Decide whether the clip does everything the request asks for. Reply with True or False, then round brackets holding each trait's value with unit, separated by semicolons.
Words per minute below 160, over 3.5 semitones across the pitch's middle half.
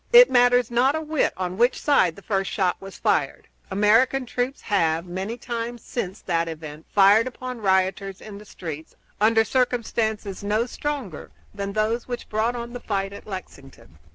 False (170 wpm; 4.2 semitones)